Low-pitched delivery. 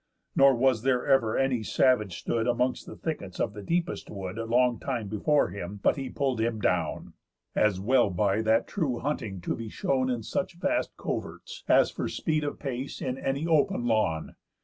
Yes: low, 120 Hz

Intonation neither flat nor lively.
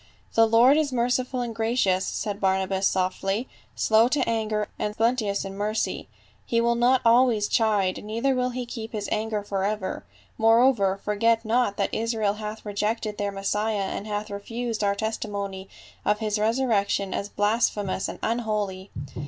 No: narrow, 2.3 semitones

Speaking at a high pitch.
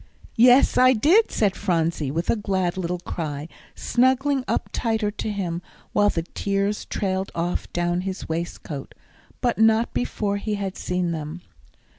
Yes: high, 195 Hz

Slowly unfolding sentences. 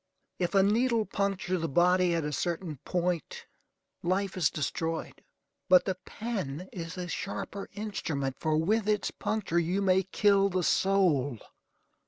No: average, 145 wpm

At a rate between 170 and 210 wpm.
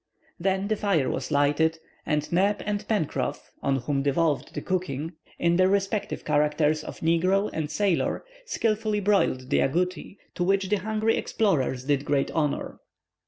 No: average, 155 wpm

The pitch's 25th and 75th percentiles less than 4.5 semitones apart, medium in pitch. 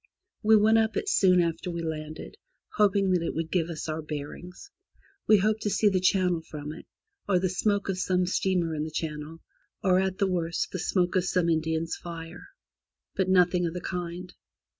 Yes: narrow, 2.6 semitones; medium, 180 Hz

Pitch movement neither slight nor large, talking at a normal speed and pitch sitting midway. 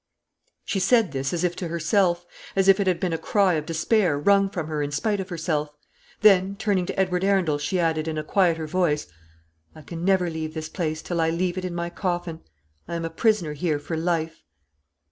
No: average, 3.0 semitones; fast, 215 wpm; medium, 175 Hz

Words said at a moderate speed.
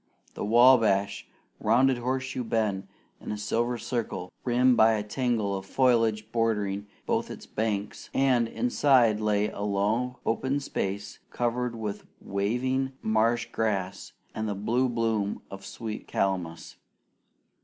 No: slow, 130 wpm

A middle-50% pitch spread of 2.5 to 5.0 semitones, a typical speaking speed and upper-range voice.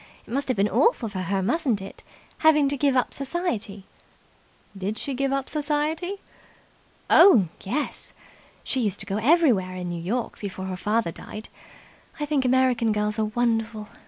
No: wide, 5.6 semitones; average, 165 wpm; high, 230 Hz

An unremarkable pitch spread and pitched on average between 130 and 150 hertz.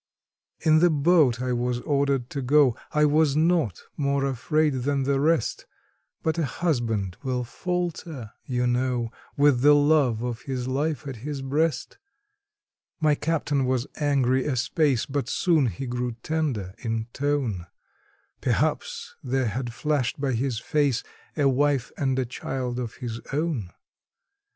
Yes: average, 3.3 semitones; low, 135 Hz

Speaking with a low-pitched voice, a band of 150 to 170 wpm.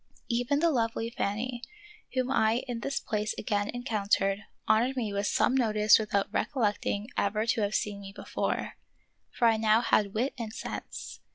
No: high, 220 Hz; average, 165 wpm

